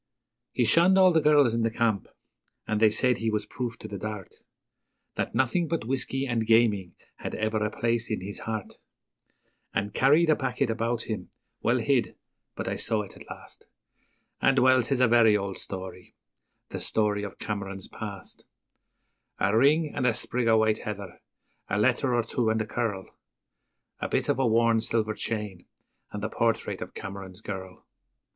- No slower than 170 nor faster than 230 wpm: Yes, average, 180 wpm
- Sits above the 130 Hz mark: No, low, 110 Hz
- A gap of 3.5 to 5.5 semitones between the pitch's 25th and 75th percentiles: No, average, 3.1 semitones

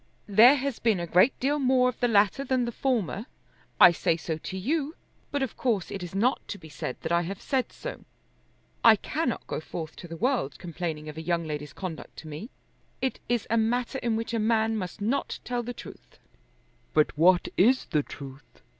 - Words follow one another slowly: No, fast, 205 wpm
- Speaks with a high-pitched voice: Yes, high, 215 Hz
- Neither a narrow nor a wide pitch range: No, wide, 6.7 semitones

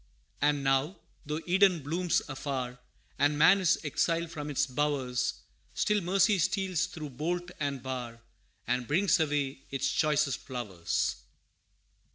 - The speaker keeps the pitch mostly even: No, average, 4.3 semitones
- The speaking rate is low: Yes, slow, 130 wpm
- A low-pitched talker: No, medium, 150 Hz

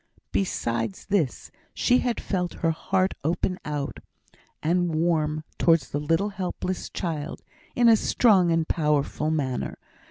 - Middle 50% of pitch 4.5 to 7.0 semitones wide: No, average, 3.7 semitones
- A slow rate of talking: Yes, slow, 130 wpm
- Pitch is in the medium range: Yes, medium, 165 Hz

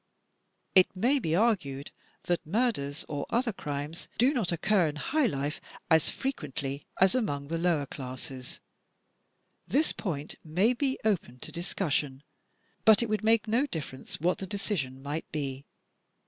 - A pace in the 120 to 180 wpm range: Yes, average, 145 wpm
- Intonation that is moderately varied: No, wide, 7.4 semitones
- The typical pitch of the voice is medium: Yes, medium, 170 Hz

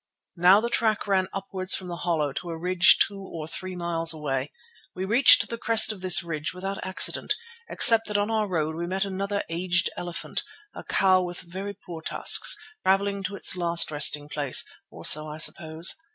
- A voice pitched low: No, medium, 185 Hz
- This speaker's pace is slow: No, average, 190 wpm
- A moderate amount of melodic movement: Yes, average, 3.0 semitones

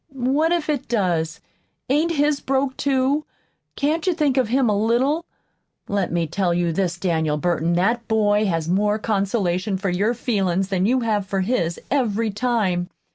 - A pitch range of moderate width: No, wide, 6.2 semitones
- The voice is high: Yes, high, 210 Hz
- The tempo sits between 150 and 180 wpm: Yes, average, 170 wpm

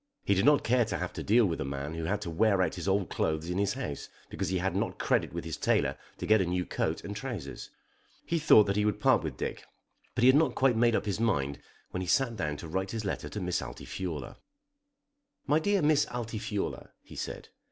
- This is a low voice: Yes, low, 100 Hz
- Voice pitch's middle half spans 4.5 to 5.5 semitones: Yes, average, 5.1 semitones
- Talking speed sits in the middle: No, fast, 240 wpm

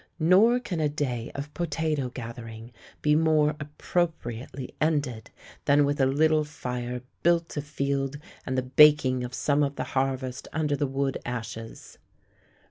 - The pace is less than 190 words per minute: Yes, average, 140 wpm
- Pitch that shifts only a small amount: No, average, 3.1 semitones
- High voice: No, medium, 140 Hz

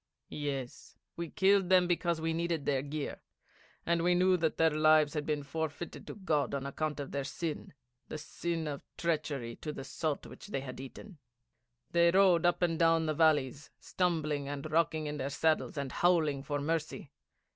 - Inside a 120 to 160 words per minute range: No, average, 180 wpm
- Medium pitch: Yes, medium, 155 Hz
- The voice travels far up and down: No, average, 2.9 semitones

